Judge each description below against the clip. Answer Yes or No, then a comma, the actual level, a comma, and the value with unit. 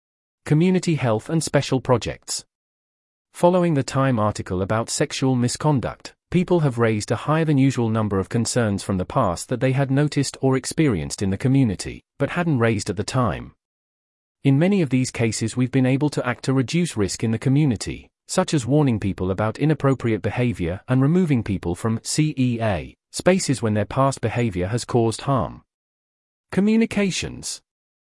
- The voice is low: Yes, low, 120 Hz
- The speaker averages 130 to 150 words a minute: No, average, 165 wpm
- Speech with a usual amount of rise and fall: No, wide, 5.7 semitones